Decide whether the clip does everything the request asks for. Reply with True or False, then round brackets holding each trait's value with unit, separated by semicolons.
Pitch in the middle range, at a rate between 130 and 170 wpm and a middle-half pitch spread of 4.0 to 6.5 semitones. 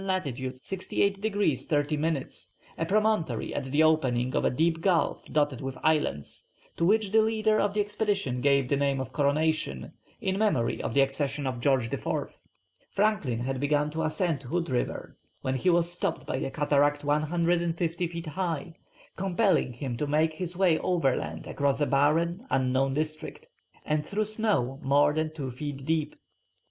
True (155 Hz; 165 wpm; 4.5 semitones)